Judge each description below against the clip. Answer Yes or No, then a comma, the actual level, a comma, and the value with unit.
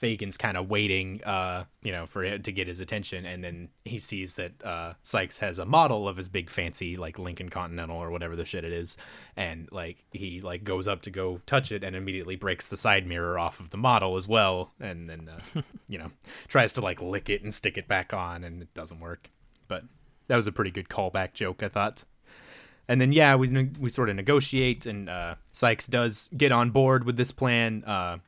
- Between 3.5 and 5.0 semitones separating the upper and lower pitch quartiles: Yes, average, 4.5 semitones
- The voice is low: Yes, very low, 95 Hz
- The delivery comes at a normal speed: No, fast, 225 wpm